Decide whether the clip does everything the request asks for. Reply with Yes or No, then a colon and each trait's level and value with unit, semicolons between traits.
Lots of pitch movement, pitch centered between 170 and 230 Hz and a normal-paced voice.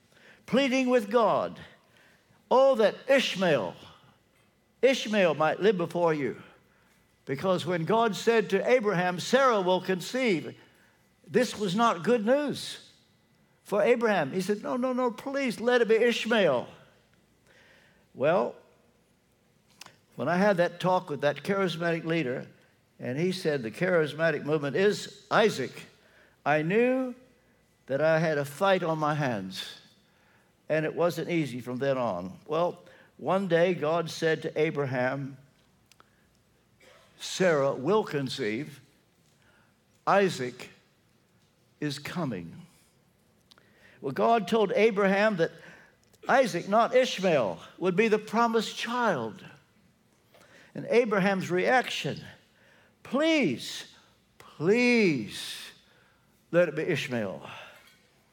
No: wide, 6.4 semitones; high, 190 Hz; slow, 110 wpm